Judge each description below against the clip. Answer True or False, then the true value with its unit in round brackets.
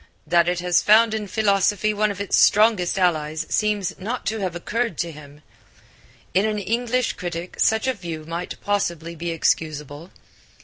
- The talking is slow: False (165 wpm)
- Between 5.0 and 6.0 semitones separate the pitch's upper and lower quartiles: False (4.1 semitones)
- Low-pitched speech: False (185 Hz)